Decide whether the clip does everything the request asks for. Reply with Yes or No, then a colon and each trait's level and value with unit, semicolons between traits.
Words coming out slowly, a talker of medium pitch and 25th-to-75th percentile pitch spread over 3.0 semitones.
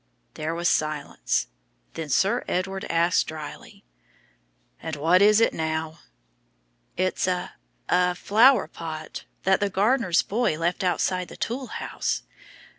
Yes: slow, 125 wpm; medium, 180 Hz; average, 3.6 semitones